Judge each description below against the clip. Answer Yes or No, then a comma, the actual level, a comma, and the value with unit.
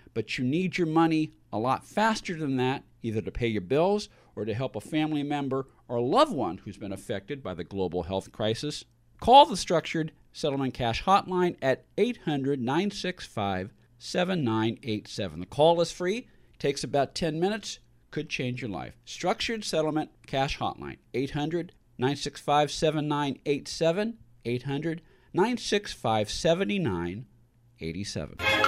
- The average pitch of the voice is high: No, low, 135 Hz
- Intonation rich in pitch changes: Yes, wide, 6.5 semitones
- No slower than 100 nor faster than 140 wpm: Yes, slow, 135 wpm